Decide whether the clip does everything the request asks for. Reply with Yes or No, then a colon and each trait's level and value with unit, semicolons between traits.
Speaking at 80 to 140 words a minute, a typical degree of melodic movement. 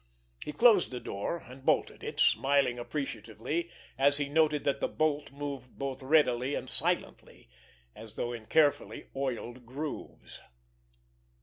Yes: slow, 135 wpm; average, 3.3 semitones